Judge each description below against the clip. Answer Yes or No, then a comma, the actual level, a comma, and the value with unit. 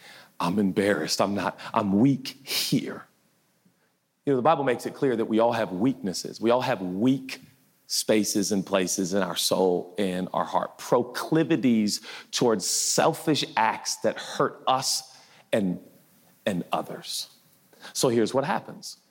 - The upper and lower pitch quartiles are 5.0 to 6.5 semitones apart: Yes, average, 5.3 semitones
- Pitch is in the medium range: No, low, 115 Hz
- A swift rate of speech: No, average, 145 wpm